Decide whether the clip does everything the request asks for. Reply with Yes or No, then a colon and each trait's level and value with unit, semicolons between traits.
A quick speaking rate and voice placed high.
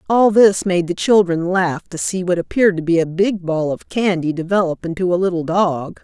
No: fast, 220 wpm; medium, 180 Hz